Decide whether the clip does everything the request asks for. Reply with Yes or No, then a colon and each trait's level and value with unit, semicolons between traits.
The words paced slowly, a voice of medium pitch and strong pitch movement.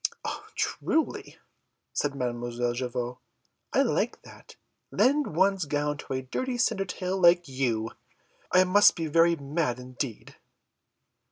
Yes: slow, 115 wpm; medium, 150 Hz; wide, 6.7 semitones